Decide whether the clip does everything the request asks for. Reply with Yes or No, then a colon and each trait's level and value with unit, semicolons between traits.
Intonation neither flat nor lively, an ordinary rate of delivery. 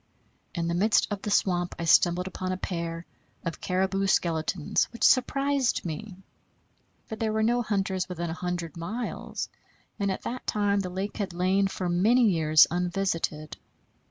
Yes: average, 3.1 semitones; average, 160 wpm